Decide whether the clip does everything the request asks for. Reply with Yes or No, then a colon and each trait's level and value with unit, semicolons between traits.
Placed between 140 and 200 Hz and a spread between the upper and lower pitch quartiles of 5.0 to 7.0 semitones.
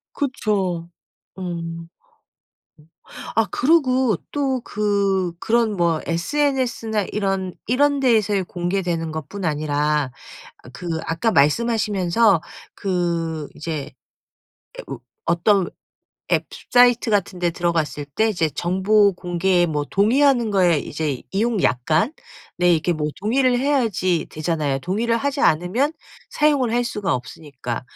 Yes: high, 190 Hz; wide, 5.6 semitones